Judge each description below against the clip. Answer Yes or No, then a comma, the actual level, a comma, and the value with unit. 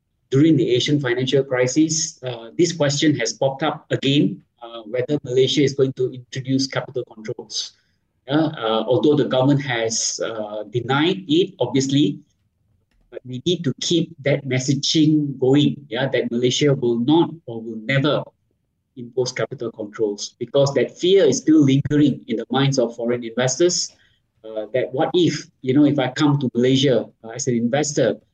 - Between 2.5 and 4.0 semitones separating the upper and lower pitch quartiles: Yes, average, 3.7 semitones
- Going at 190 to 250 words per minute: No, average, 165 wpm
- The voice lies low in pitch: Yes, low, 130 Hz